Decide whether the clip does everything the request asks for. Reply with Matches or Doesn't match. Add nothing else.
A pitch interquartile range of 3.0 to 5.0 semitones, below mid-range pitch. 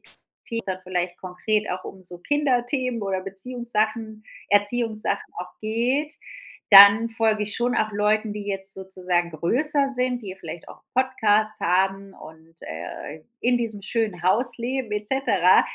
Doesn't match